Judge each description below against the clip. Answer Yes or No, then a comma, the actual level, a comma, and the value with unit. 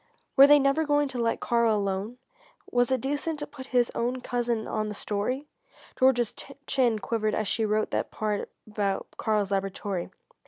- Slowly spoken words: No, average, 170 wpm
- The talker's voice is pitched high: Yes, high, 235 Hz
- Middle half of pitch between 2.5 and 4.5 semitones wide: Yes, average, 3.8 semitones